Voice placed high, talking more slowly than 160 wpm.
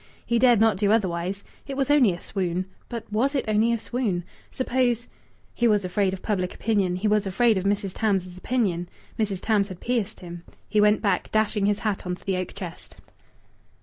No: high, 205 Hz; average, 200 wpm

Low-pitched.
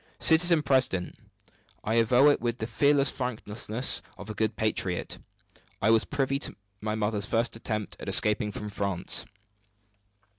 Yes: low, 115 Hz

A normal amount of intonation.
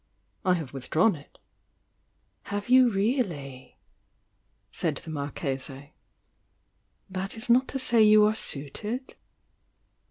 No: wide, 7.9 semitones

